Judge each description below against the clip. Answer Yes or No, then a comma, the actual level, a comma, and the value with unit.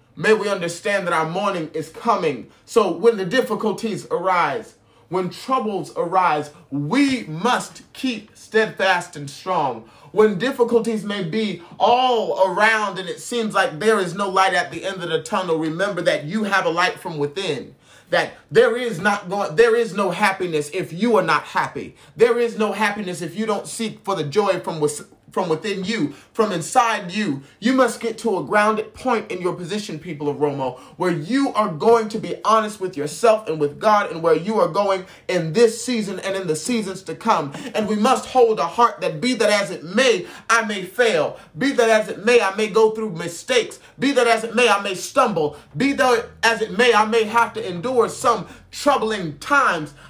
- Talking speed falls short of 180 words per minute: No, average, 200 wpm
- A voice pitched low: No, high, 210 Hz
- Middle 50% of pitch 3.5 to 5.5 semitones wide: Yes, average, 4.5 semitones